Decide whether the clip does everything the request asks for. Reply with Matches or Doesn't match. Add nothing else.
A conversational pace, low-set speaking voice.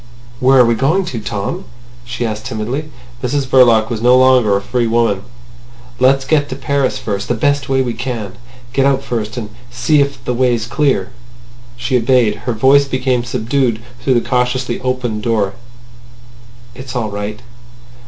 Matches